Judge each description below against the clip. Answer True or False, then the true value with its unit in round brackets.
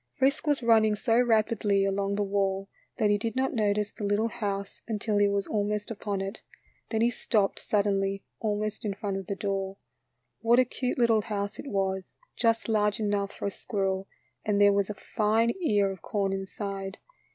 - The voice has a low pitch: False (205 Hz)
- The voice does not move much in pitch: True (2.0 semitones)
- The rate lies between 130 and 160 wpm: False (190 wpm)